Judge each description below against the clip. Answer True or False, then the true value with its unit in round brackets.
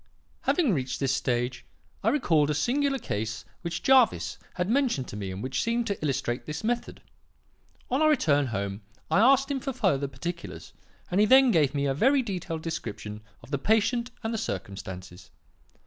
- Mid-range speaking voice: True (165 Hz)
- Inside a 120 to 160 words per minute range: False (180 wpm)